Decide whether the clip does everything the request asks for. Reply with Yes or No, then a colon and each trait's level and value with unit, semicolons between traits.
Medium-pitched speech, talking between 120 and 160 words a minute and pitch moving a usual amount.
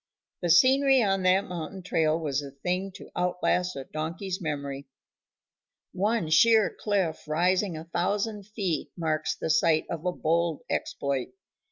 Yes: medium, 175 Hz; average, 150 wpm; average, 3.8 semitones